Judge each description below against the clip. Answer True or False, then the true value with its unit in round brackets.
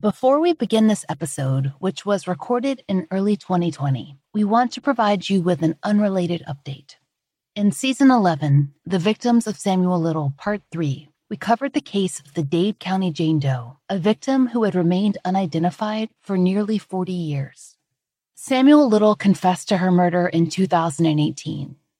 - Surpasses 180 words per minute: False (160 wpm)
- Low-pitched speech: False (185 Hz)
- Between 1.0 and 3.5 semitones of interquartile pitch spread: False (4.9 semitones)